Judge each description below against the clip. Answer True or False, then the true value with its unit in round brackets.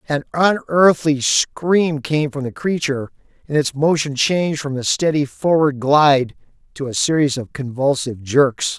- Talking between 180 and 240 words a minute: False (150 wpm)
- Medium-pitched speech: True (145 Hz)